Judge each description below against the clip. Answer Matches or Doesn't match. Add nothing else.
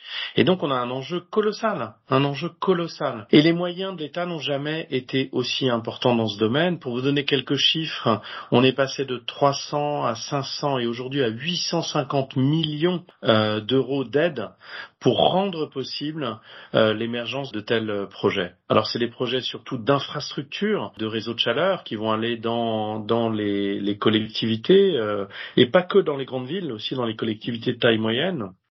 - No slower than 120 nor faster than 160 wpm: Doesn't match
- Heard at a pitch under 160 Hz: Matches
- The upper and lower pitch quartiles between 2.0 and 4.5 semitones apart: Doesn't match